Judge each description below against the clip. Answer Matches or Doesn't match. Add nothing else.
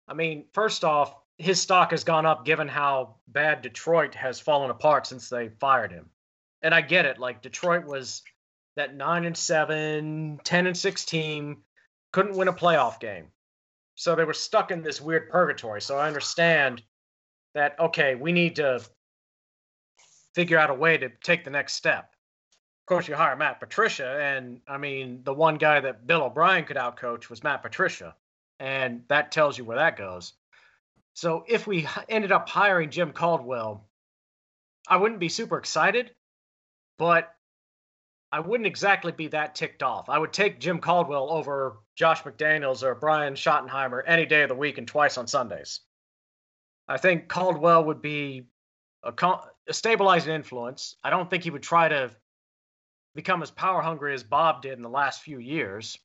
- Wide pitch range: Doesn't match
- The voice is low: Doesn't match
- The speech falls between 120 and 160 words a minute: Doesn't match